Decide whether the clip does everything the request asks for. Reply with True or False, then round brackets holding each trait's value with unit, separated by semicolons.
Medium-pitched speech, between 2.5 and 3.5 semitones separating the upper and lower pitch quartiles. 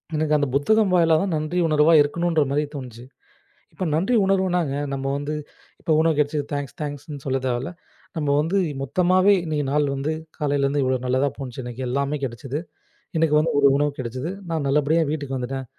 True (145 Hz; 3.0 semitones)